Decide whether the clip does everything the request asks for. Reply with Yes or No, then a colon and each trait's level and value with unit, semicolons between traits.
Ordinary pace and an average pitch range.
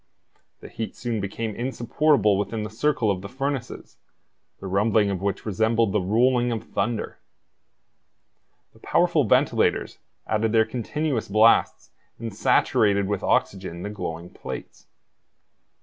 No: slow, 125 wpm; average, 3.0 semitones